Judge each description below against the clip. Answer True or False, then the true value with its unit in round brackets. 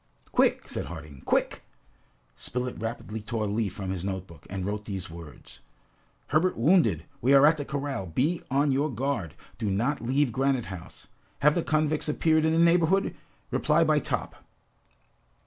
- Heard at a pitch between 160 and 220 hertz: False (125 Hz)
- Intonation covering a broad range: True (7.4 semitones)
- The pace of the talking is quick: False (165 wpm)